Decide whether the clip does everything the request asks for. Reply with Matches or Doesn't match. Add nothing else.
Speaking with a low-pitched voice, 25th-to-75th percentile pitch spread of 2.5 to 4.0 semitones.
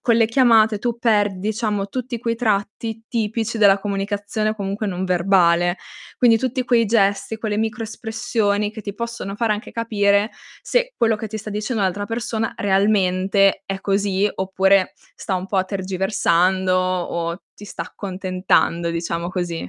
Doesn't match